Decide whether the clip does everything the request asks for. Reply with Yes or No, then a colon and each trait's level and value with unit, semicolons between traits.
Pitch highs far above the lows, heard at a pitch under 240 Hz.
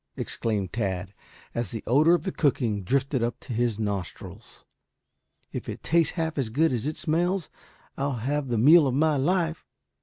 Yes: wide, 5.8 semitones; low, 135 Hz